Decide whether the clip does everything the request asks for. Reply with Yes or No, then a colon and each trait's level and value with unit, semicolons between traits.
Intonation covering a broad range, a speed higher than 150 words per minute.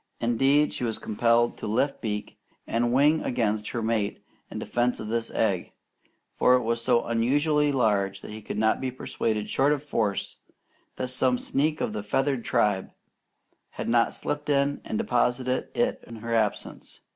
No: average, 3.6 semitones; average, 170 wpm